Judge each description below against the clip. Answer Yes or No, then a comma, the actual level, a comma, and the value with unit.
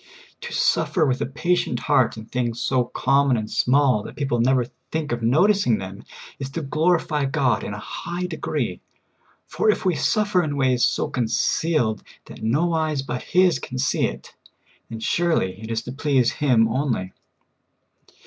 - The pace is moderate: Yes, average, 170 wpm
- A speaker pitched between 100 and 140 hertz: Yes, low, 135 Hz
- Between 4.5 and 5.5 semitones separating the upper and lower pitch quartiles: Yes, average, 5.1 semitones